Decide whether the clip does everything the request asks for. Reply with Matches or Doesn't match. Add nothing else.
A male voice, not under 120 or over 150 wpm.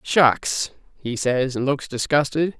Matches